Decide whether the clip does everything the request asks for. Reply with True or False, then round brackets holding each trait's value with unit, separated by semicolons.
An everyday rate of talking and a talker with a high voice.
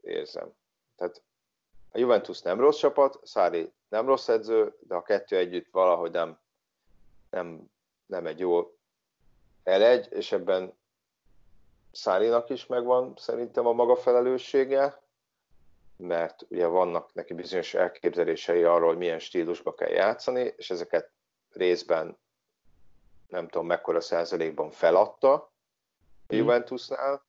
True (115 wpm; 390 Hz)